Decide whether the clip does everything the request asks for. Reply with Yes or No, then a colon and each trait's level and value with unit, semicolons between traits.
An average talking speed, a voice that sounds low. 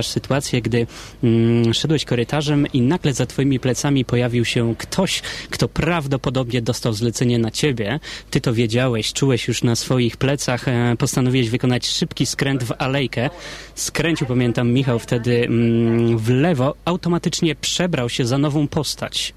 Yes: average, 145 wpm; low, 125 Hz